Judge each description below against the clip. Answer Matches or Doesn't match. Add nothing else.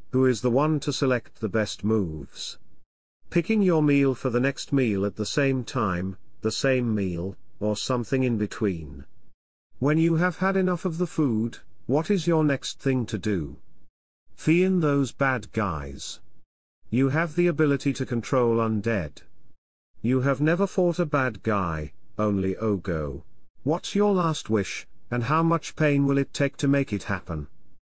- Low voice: Matches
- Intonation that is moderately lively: Doesn't match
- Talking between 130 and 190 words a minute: Matches